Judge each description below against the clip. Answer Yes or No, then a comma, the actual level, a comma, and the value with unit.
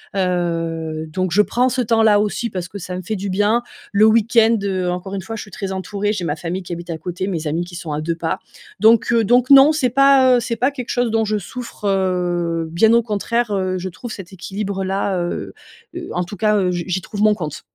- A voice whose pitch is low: No, high, 195 Hz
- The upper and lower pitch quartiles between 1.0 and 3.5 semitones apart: No, average, 4.1 semitones